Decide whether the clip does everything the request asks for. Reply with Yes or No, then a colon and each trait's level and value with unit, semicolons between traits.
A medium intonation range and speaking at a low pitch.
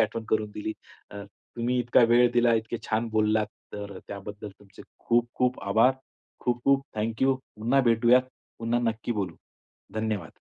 No: narrow, 2.2 semitones; low, 115 Hz